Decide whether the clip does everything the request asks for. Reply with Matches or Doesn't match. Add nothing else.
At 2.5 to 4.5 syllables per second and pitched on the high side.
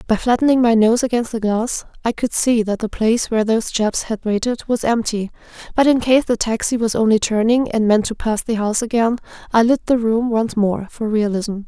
Doesn't match